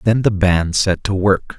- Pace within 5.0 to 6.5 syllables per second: No, 4.1 syllables/s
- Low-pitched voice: Yes, very low, 95 Hz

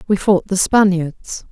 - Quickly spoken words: No, average, 160 wpm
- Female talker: Yes, female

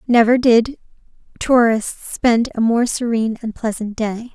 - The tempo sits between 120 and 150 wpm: Yes, average, 140 wpm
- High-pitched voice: Yes, high, 230 Hz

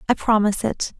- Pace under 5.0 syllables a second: No, 6.5 syllables/s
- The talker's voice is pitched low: No, high, 215 Hz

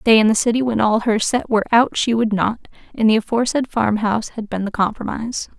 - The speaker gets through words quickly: Yes, fast, 225 wpm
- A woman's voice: Yes, female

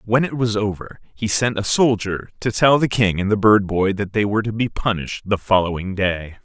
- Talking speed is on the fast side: Yes, fast, 235 wpm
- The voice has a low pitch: Yes, low, 105 Hz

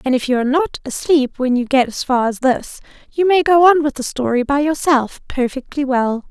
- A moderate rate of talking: No, fast, 230 wpm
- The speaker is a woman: Yes, female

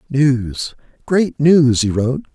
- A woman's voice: No, male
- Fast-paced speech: No, slow, 130 wpm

